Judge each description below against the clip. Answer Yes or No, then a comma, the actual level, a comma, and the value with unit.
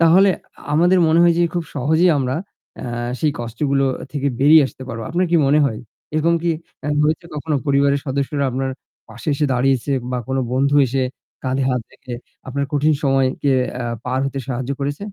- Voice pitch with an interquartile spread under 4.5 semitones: Yes, average, 3.0 semitones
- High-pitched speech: No, medium, 140 Hz